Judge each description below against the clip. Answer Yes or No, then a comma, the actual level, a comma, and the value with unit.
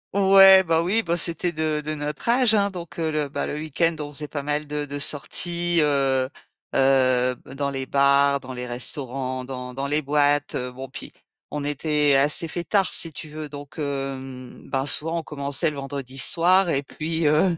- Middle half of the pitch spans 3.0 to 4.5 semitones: Yes, average, 3.3 semitones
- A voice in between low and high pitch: Yes, medium, 145 Hz